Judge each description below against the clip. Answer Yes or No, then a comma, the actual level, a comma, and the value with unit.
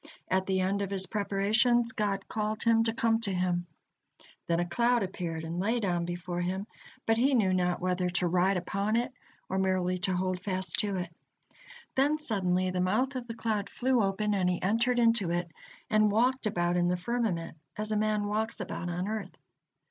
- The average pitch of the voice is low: No, high, 195 Hz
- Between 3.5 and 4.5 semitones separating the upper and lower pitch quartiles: Yes, average, 3.8 semitones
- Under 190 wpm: No, average, 195 wpm